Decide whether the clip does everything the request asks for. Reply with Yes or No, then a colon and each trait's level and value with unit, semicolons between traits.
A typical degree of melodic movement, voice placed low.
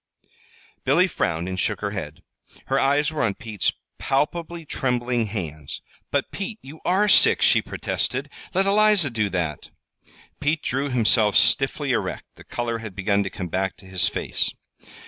No: wide, 7.8 semitones; low, 115 Hz